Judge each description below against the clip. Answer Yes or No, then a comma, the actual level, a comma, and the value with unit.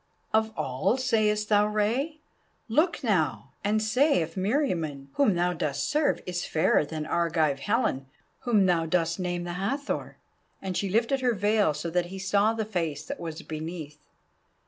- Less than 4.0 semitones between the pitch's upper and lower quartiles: No, average, 5.2 semitones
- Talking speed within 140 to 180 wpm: Yes, average, 165 wpm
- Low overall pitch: No, high, 190 Hz